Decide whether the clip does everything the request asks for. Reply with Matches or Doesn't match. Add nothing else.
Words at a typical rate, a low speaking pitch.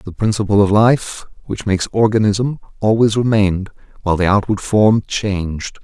Matches